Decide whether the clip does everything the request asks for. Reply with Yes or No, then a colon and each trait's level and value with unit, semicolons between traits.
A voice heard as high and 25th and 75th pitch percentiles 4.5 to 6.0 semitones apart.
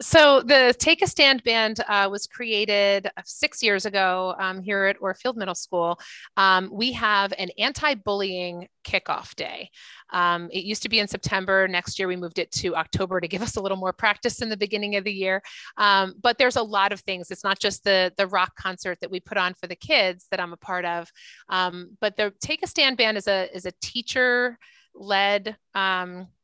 No: high, 200 Hz; average, 2.9 semitones